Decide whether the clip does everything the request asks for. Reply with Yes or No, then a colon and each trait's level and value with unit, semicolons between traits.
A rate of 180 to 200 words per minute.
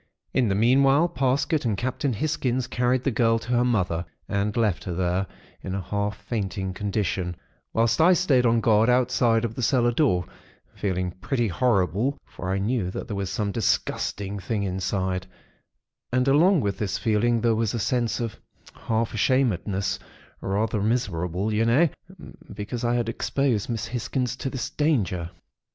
No: average, 165 wpm